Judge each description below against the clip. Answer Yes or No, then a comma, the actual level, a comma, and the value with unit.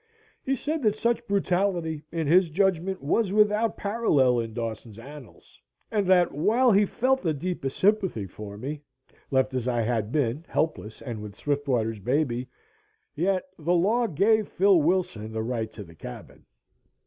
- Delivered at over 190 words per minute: No, average, 160 wpm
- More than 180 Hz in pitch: No, medium, 155 Hz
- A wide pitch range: Yes, wide, 8.7 semitones